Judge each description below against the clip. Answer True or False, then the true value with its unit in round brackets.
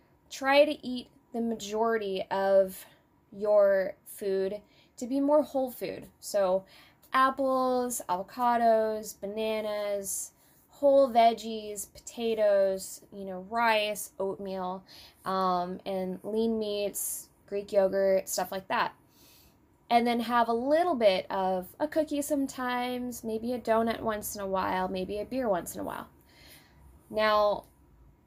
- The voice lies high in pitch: True (215 Hz)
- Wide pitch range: False (4.2 semitones)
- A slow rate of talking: True (125 wpm)